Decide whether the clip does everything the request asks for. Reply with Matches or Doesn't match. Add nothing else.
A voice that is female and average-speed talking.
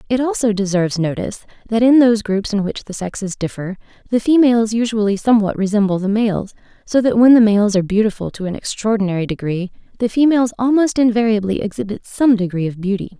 Matches